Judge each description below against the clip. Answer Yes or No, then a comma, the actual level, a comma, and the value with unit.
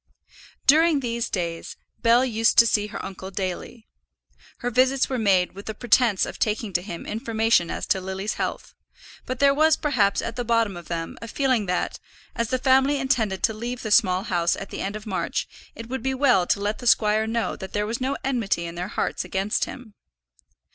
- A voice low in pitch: No, high, 220 Hz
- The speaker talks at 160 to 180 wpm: No, fast, 205 wpm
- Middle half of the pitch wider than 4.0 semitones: Yes, average, 4.4 semitones